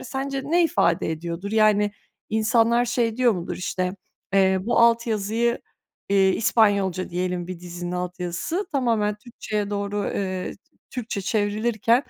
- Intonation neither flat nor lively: Yes, average, 4.1 semitones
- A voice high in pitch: Yes, high, 210 Hz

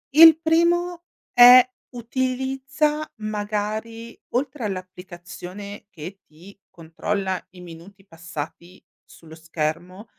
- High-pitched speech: Yes, high, 205 Hz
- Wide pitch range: Yes, wide, 6.2 semitones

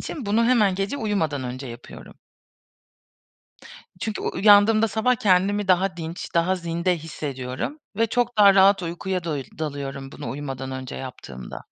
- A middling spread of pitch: No, wide, 6.6 semitones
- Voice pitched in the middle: Yes, medium, 180 Hz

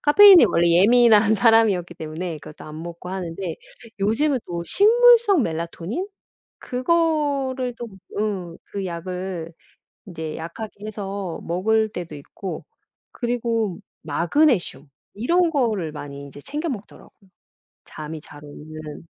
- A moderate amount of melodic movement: No, wide, 6.7 semitones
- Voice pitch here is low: No, high, 195 Hz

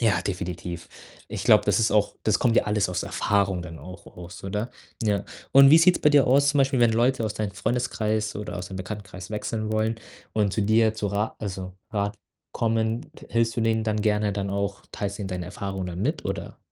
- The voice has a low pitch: Yes, low, 105 Hz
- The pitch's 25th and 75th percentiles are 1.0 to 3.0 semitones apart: Yes, average, 2.7 semitones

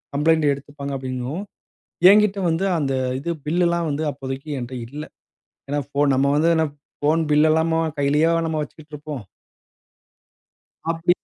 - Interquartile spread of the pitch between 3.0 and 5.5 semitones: No, narrow, 2.6 semitones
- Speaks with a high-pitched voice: No, medium, 150 Hz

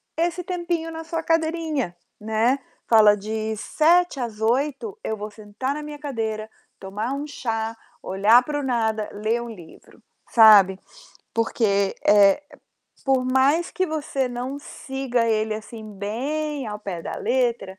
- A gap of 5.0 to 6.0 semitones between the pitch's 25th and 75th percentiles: Yes, wide, 5.4 semitones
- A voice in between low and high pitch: No, high, 240 Hz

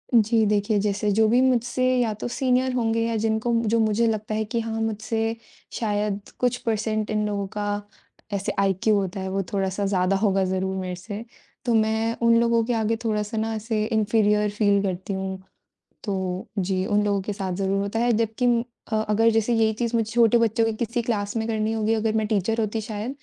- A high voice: Yes, high, 215 Hz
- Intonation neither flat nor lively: No, narrow, 2.0 semitones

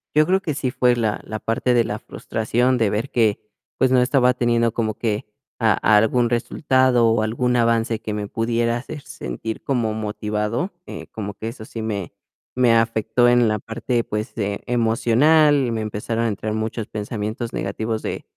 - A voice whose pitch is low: Yes, low, 115 Hz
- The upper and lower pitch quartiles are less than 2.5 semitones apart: Yes, narrow, 2.1 semitones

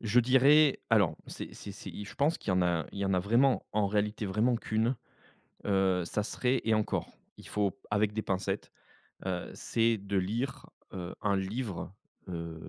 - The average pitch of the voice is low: Yes, low, 105 Hz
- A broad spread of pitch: No, average, 3.3 semitones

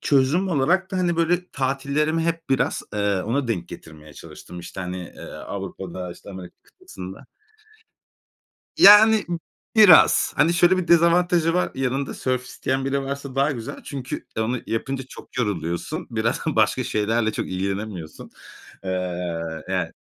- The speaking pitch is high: No, low, 130 Hz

